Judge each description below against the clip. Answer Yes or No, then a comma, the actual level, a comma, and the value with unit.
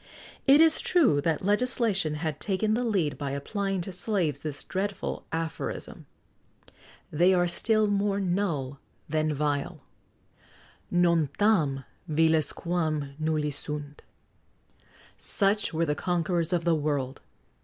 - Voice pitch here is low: No, medium, 170 Hz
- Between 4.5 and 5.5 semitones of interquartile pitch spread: Yes, average, 4.8 semitones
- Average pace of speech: No, slow, 125 wpm